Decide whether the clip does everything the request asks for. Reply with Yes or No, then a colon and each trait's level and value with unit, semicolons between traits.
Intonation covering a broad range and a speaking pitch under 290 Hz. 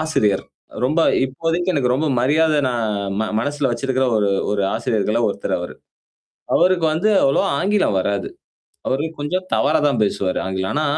Yes: wide, 6.3 semitones; low, 135 Hz